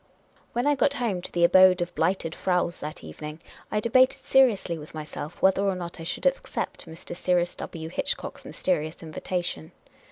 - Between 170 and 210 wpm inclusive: Yes, average, 180 wpm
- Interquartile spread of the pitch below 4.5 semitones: Yes, average, 3.8 semitones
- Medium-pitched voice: Yes, medium, 180 Hz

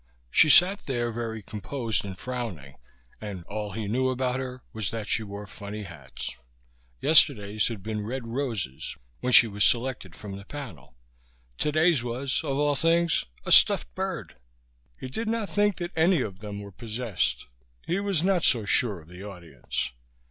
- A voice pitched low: Yes, low, 115 Hz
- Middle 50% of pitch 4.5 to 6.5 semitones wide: Yes, average, 5.3 semitones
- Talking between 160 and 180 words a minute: Yes, average, 170 wpm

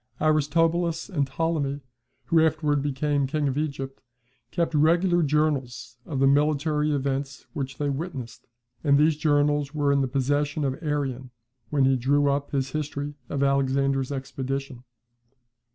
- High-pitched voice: No, medium, 145 Hz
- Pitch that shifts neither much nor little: No, narrow, 1.9 semitones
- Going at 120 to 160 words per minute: Yes, average, 140 wpm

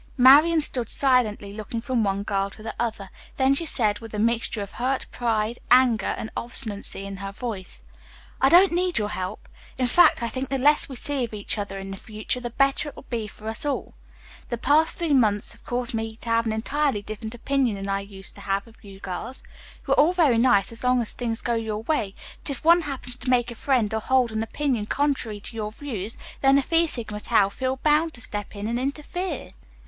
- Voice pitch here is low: No, high, 235 Hz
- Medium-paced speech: No, fast, 225 wpm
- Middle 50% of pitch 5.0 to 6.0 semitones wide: No, average, 4.3 semitones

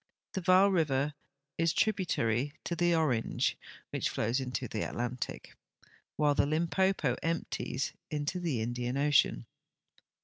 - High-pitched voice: No, medium, 145 Hz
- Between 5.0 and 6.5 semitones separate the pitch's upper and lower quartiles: Yes, wide, 5.4 semitones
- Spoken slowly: Yes, slow, 130 wpm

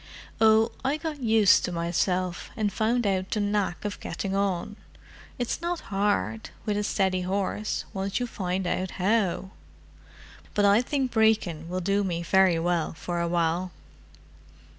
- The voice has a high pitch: Yes, high, 195 Hz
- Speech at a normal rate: Yes, average, 145 wpm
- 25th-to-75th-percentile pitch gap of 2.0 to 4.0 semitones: Yes, average, 3.4 semitones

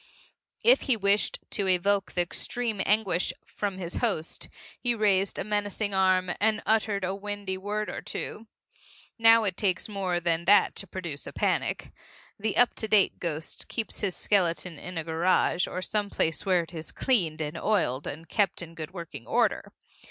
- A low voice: No, high, 190 Hz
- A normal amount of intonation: Yes, average, 3.3 semitones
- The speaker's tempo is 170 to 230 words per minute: Yes, average, 180 wpm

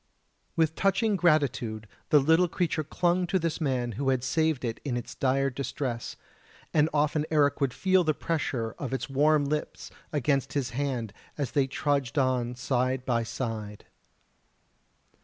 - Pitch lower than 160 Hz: Yes, medium, 140 Hz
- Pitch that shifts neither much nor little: Yes, average, 3.8 semitones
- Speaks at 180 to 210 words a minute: No, average, 155 wpm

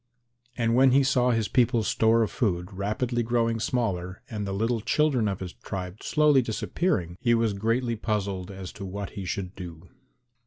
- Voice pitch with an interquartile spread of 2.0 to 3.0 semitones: No, average, 3.8 semitones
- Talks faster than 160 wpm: Yes, average, 180 wpm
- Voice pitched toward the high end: No, low, 110 Hz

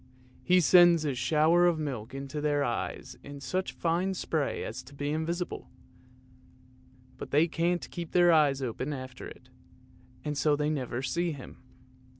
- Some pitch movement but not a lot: Yes, average, 3.7 semitones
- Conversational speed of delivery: Yes, average, 155 wpm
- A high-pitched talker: No, medium, 150 Hz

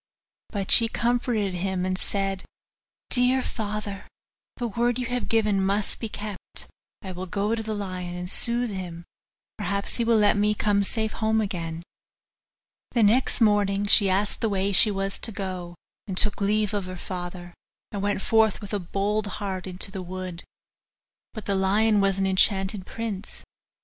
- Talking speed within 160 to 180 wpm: Yes, average, 170 wpm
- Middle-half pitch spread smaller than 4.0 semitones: Yes, narrow, 2.4 semitones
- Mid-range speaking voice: No, high, 200 Hz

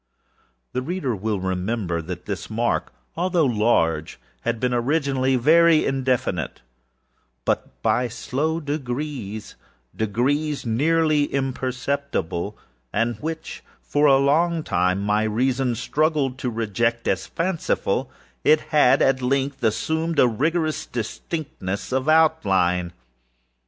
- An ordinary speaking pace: No, slow, 105 wpm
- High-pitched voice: No, low, 130 Hz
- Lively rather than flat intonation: Yes, wide, 5.7 semitones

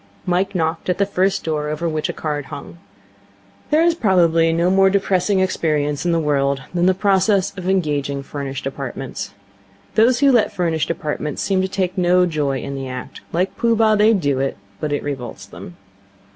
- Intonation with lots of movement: No, average, 4.7 semitones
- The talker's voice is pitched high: No, medium, 170 Hz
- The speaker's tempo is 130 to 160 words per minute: No, average, 185 wpm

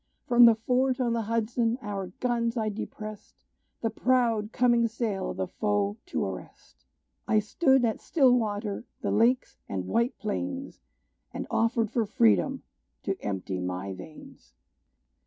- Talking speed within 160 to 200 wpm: No, average, 140 wpm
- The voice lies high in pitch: Yes, high, 225 Hz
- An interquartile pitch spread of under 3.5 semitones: Yes, average, 3.0 semitones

